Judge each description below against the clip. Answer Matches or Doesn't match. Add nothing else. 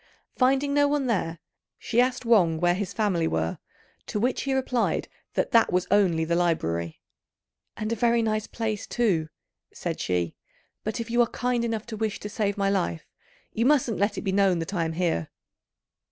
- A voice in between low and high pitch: Doesn't match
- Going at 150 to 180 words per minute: Doesn't match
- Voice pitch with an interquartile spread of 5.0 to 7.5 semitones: Matches